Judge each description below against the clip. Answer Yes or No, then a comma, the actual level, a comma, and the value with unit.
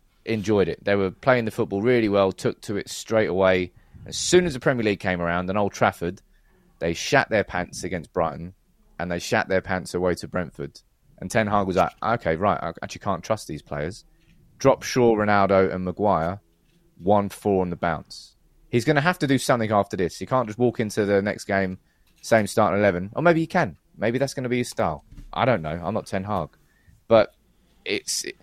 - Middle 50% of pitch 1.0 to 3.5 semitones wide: No, average, 4.4 semitones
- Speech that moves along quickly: Yes, fast, 220 wpm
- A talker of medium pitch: No, low, 100 Hz